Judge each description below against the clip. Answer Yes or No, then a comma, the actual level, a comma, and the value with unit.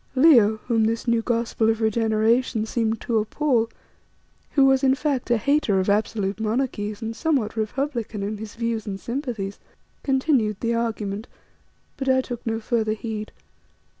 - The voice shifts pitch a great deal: No, average, 2.9 semitones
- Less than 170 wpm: Yes, average, 155 wpm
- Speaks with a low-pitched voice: No, high, 225 Hz